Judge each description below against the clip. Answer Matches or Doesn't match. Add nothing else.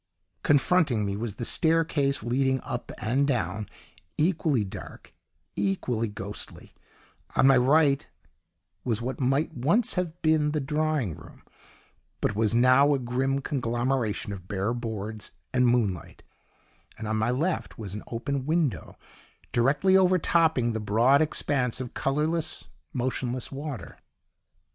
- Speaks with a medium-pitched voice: Doesn't match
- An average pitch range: Matches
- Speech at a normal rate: Doesn't match